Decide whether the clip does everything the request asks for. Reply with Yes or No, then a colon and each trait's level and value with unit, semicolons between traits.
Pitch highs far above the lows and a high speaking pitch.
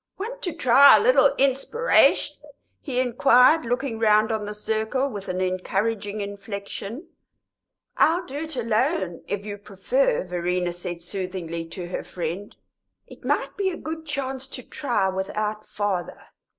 Yes: wide, 6.4 semitones; high, 220 Hz